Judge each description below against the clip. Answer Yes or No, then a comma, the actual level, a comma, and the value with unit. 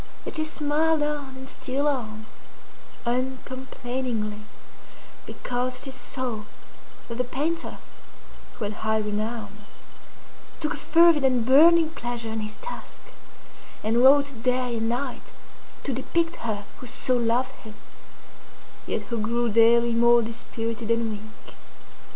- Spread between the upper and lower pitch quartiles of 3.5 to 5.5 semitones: No, average, 3.0 semitones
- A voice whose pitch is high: Yes, high, 245 Hz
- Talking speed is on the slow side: Yes, slow, 125 wpm